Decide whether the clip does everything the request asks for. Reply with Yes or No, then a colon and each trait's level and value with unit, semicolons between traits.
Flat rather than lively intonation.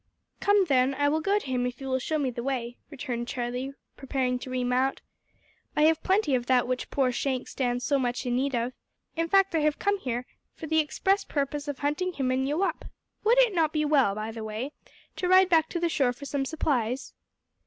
No: average, 4.1 semitones